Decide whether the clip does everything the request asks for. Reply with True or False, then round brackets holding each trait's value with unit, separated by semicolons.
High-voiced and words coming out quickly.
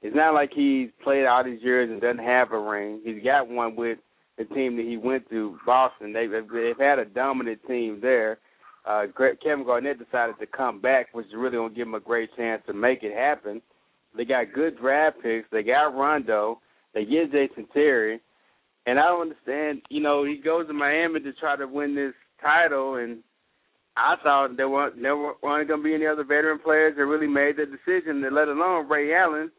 False (135 Hz; 210 wpm)